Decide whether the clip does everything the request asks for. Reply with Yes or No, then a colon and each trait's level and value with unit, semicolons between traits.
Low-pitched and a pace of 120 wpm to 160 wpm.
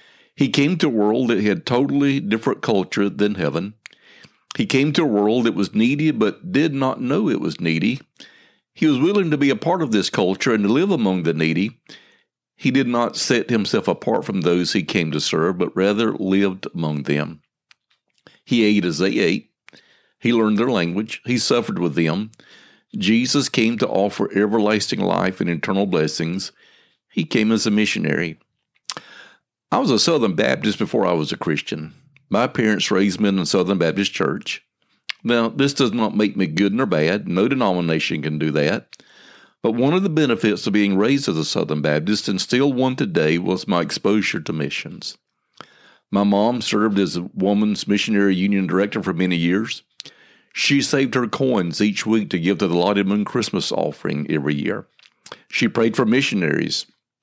No: low, 105 Hz; average, 180 wpm